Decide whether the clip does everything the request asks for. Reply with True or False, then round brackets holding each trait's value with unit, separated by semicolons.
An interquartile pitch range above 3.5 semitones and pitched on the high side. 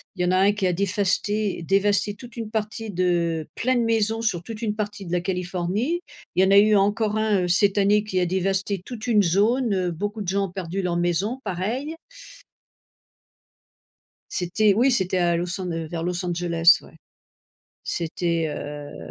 False (3.2 semitones; 195 Hz)